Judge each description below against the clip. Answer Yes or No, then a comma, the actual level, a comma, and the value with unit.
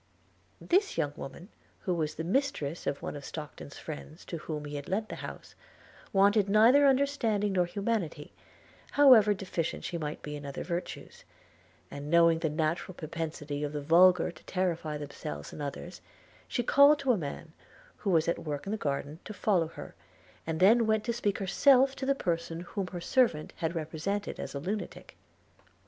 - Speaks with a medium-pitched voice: Yes, medium, 175 Hz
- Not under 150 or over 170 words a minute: No, average, 180 wpm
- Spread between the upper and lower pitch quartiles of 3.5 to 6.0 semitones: Yes, wide, 5.6 semitones